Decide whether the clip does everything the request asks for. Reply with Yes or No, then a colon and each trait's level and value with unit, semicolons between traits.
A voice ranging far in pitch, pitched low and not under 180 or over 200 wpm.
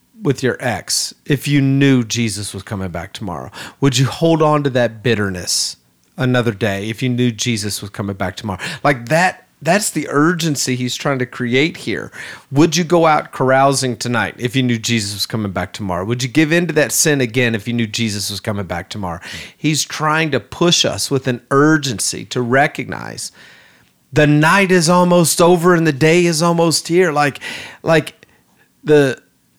Yes: wide, 5.7 semitones; low, 130 Hz; average, 185 wpm